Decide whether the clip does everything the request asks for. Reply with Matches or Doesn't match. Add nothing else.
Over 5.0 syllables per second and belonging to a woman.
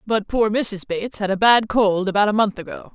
Matches